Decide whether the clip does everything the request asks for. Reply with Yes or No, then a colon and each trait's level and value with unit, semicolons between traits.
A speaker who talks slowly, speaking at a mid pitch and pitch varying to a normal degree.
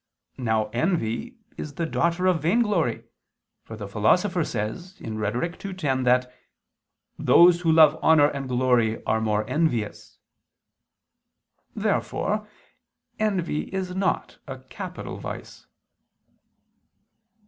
No: slow, 105 wpm; medium, 150 Hz; wide, 7.9 semitones